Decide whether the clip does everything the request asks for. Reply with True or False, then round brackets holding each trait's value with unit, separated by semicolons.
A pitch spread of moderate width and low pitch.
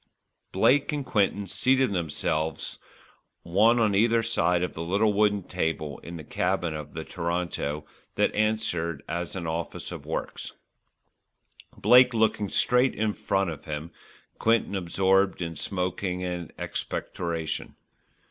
True (4.3 semitones; 90 Hz)